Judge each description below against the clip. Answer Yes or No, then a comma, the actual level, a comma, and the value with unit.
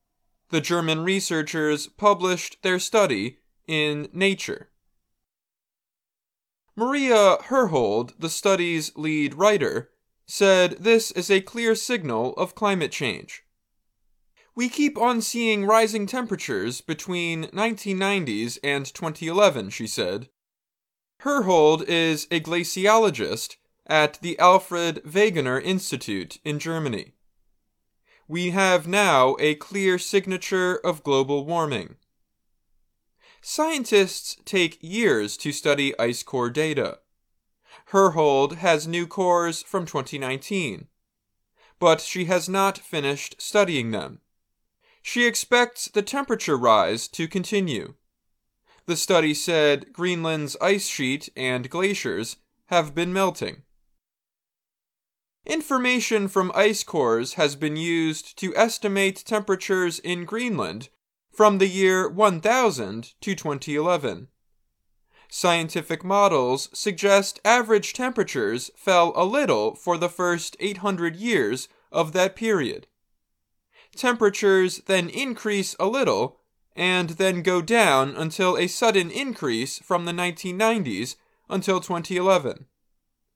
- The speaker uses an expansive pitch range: No, average, 4.6 semitones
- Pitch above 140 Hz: Yes, medium, 185 Hz